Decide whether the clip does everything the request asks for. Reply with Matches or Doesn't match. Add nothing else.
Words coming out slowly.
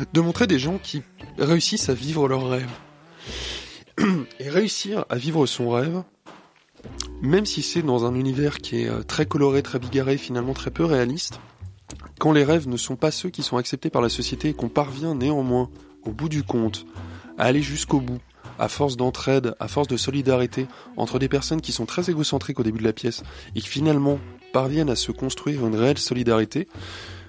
Doesn't match